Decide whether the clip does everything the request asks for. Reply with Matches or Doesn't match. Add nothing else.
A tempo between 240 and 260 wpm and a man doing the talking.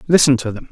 Matches